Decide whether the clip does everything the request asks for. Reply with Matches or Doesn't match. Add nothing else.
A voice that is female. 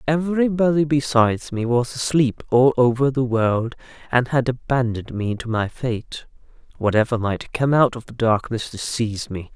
Doesn't match